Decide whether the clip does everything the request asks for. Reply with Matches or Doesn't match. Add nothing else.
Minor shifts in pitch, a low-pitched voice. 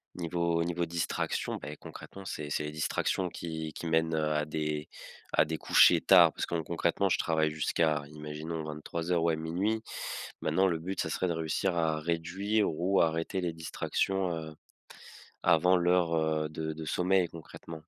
Matches